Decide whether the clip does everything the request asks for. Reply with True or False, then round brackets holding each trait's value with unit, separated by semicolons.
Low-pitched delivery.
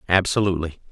True (90 Hz)